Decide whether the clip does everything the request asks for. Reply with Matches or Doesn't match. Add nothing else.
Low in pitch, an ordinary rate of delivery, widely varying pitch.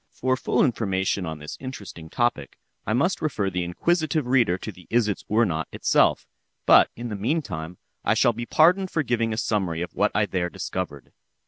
Matches